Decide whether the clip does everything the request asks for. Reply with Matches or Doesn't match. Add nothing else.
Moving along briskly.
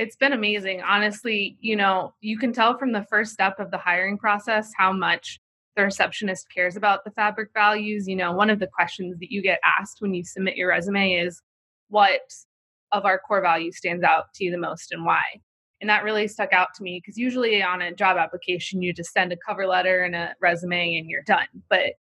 Matches